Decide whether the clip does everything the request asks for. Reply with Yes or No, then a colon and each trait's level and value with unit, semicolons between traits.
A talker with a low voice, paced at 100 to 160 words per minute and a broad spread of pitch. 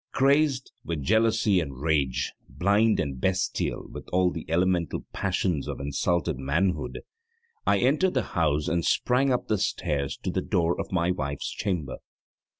Yes: very low, 90 Hz; average, 150 wpm; wide, 6.3 semitones